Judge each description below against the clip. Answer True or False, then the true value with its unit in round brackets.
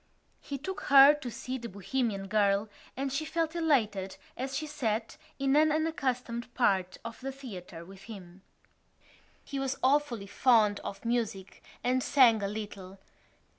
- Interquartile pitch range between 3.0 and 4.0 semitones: False (5.4 semitones)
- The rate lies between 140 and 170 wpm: True (150 wpm)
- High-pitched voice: True (240 Hz)